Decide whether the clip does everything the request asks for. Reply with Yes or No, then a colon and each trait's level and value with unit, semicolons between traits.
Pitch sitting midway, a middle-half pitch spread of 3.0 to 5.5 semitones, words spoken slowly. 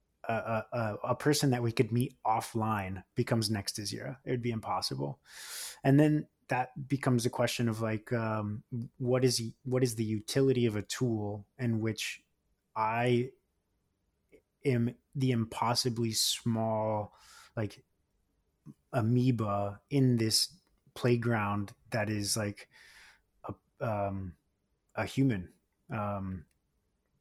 No: low, 115 Hz; average, 3.4 semitones; slow, 120 wpm